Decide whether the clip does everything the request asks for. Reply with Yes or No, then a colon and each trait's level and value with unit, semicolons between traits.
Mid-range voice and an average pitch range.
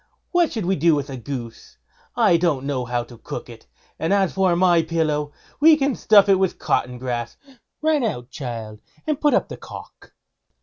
No: medium, 160 Hz; wide, 7.8 semitones